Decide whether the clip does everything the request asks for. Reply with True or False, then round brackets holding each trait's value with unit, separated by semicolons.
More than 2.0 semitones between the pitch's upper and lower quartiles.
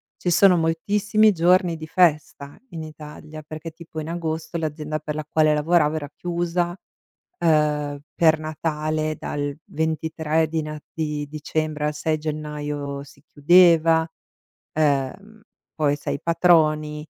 False (1.7 semitones)